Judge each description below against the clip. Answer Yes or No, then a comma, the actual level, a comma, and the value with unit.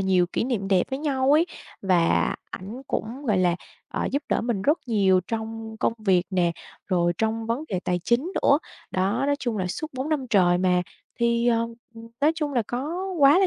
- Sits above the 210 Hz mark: Yes, high, 225 Hz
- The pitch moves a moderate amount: No, wide, 6.1 semitones